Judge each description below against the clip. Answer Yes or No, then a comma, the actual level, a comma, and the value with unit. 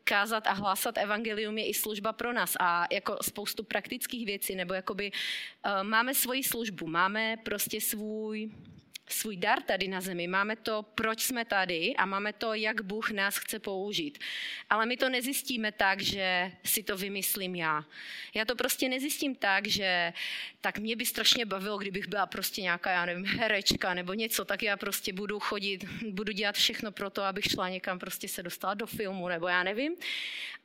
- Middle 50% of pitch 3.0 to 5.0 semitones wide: No, narrow, 2.5 semitones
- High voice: Yes, high, 205 Hz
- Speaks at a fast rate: Yes, fast, 180 wpm